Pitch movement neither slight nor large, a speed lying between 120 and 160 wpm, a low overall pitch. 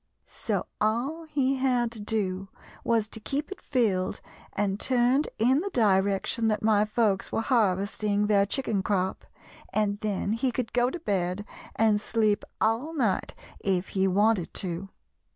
No: average, 3.6 semitones; average, 150 wpm; high, 215 Hz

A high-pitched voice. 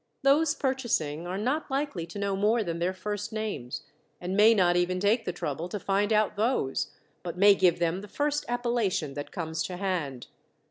Yes: high, 195 Hz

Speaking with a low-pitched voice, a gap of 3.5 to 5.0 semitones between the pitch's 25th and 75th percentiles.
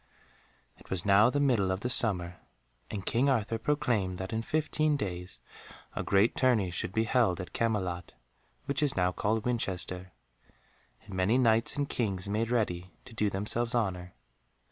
Yes: low, 105 Hz; average, 4.4 semitones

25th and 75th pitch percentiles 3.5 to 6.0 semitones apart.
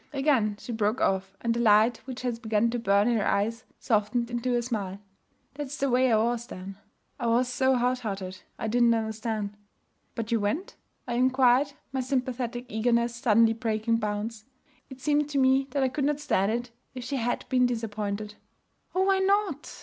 No: average, 2.9 semitones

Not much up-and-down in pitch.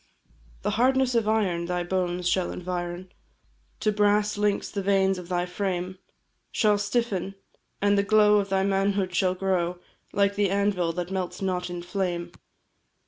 Yes: narrow, 2.3 semitones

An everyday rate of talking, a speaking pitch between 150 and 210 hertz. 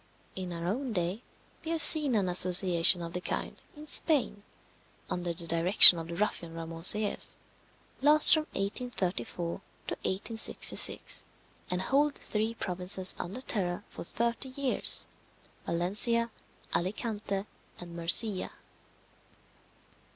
No: slow, 120 wpm; high, 190 Hz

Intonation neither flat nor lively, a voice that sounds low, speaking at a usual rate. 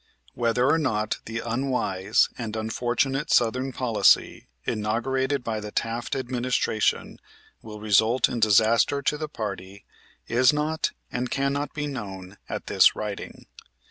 No: average, 3.5 semitones; low, 120 Hz; slow, 130 wpm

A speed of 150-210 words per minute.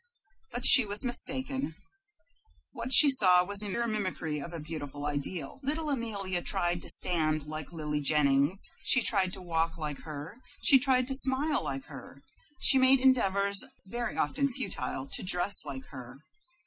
Yes: average, 160 wpm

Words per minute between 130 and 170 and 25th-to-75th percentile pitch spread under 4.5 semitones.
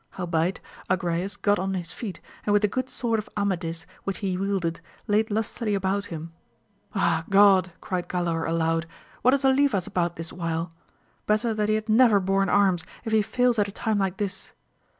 No: average, 185 wpm; average, 3.5 semitones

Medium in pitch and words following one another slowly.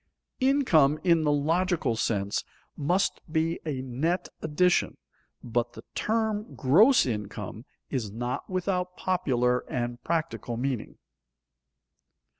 Yes: medium, 150 Hz; slow, 105 wpm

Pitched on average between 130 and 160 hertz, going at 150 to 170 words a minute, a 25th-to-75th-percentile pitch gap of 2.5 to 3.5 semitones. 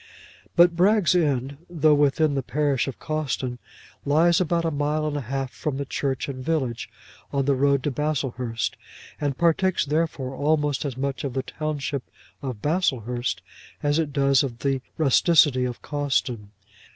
Yes: medium, 140 Hz; average, 160 wpm; average, 2.8 semitones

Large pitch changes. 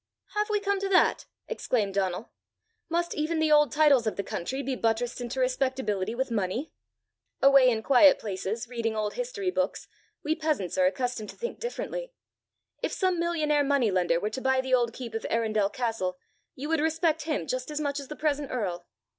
Yes: wide, 5.8 semitones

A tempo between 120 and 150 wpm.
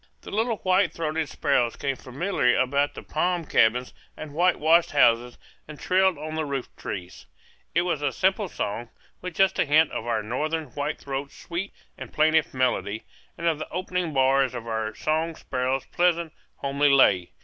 No: average, 170 wpm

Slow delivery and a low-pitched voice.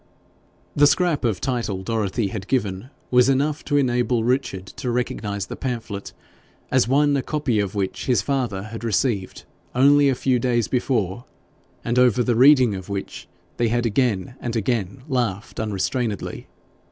No: average, 155 wpm; low, 120 Hz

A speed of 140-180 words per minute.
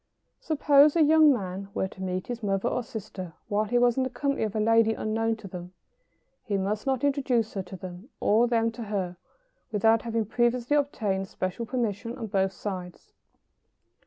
No: average, 190 wpm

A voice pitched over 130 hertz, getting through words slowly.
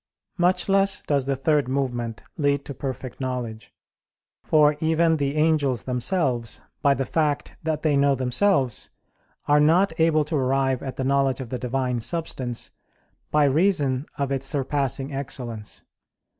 No: medium, 140 Hz; average, 145 wpm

